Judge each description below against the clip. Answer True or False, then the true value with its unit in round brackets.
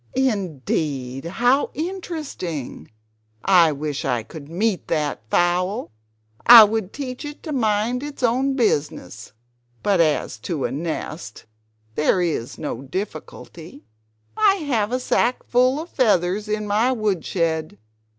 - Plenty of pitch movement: True (8.0 semitones)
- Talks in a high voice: True (200 Hz)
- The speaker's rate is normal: False (125 wpm)